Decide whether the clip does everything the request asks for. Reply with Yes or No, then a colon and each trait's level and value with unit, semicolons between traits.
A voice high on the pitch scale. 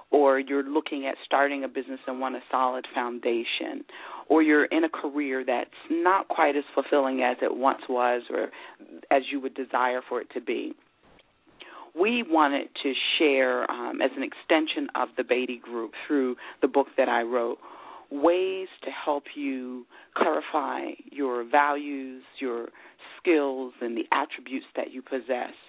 No: low, 135 Hz